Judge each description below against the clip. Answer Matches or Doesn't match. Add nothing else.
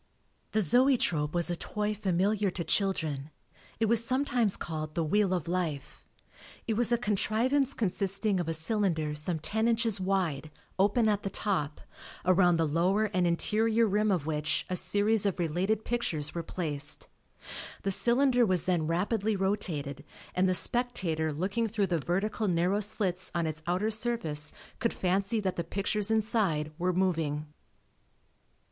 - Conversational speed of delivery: Matches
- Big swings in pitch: Doesn't match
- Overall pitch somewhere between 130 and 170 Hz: Doesn't match